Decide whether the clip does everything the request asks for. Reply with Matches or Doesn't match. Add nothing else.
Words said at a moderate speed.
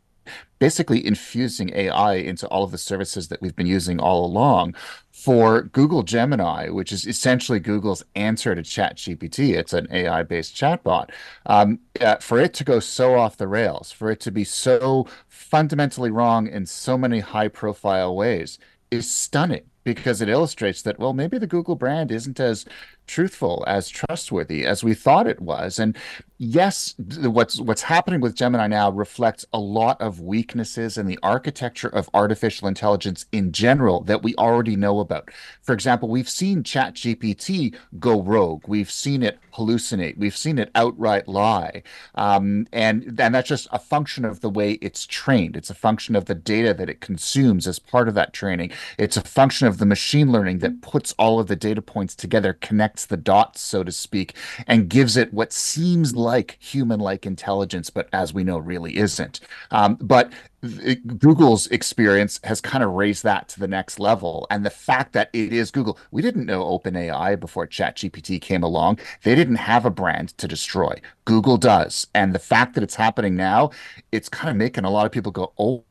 Matches